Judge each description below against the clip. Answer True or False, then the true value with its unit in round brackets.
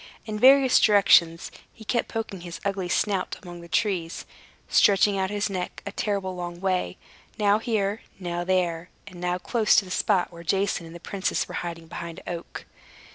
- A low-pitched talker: False (185 Hz)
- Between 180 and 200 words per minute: True (185 wpm)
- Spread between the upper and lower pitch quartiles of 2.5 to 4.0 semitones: True (2.9 semitones)